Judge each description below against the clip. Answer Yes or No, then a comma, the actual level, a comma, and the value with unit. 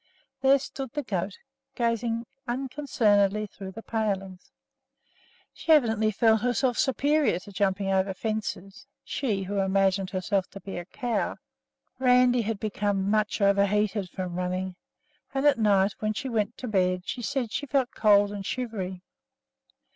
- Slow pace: No, average, 145 wpm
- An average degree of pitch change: Yes, average, 3.8 semitones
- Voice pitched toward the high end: Yes, high, 210 Hz